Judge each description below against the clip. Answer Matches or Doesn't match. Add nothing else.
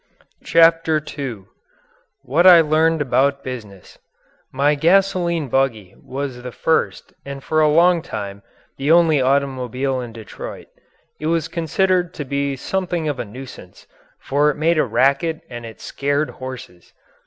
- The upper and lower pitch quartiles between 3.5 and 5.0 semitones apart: Matches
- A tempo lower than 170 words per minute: Matches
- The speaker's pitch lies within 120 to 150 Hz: Matches